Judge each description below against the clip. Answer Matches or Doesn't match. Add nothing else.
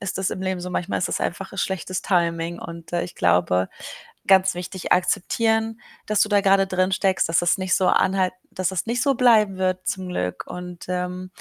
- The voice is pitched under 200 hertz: Matches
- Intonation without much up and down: Matches